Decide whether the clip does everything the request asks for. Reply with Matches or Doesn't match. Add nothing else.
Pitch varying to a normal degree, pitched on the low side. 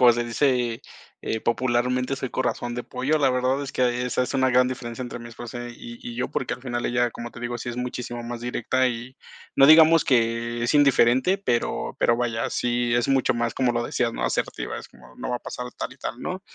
Doesn't match